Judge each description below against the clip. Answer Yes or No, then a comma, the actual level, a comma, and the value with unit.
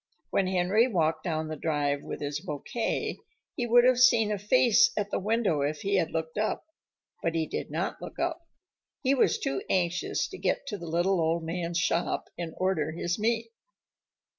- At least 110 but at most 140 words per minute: No, average, 190 wpm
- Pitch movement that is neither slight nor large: No, wide, 5.7 semitones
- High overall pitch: No, medium, 180 Hz